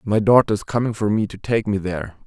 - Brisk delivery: Yes, fast, 265 wpm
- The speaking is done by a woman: No, male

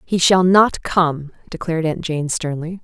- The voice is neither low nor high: Yes, medium, 170 Hz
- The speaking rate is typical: Yes, average, 170 wpm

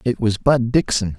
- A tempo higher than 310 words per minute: No, fast, 205 wpm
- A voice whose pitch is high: No, low, 115 Hz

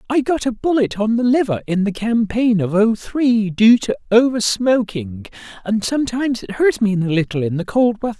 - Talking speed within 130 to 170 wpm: No, fast, 205 wpm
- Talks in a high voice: Yes, high, 220 Hz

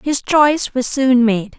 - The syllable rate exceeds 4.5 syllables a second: No, 4.1 syllables/s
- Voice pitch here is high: Yes, very high, 255 Hz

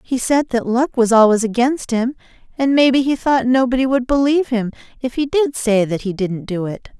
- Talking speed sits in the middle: No, fast, 215 wpm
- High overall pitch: Yes, high, 245 Hz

